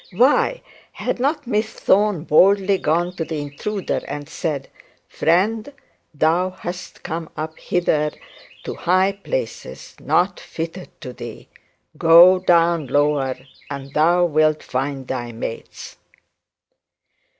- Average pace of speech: No, slow, 115 wpm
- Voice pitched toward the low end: No, medium, 170 Hz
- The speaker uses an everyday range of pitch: Yes, average, 4.1 semitones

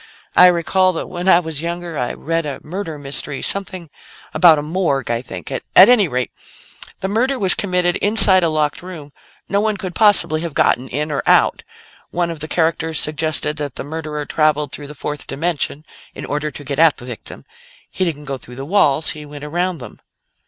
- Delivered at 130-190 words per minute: No, average, 200 wpm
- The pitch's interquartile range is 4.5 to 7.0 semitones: No, average, 3.6 semitones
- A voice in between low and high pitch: Yes, medium, 160 Hz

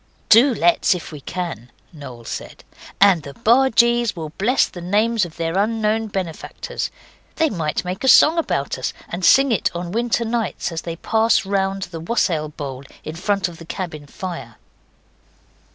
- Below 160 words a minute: No, average, 170 wpm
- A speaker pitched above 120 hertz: Yes, medium, 185 Hz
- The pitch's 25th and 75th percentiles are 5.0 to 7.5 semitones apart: Yes, wide, 5.4 semitones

